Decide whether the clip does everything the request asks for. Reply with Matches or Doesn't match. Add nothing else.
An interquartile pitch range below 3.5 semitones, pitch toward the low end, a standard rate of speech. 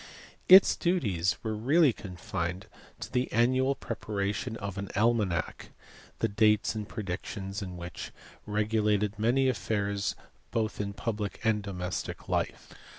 Doesn't match